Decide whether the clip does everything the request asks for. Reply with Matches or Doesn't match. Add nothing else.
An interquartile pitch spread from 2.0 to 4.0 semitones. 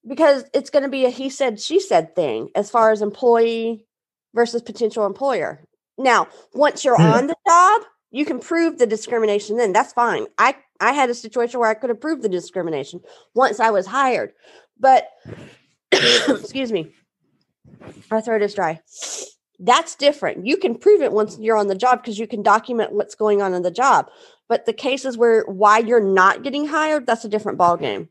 Doesn't match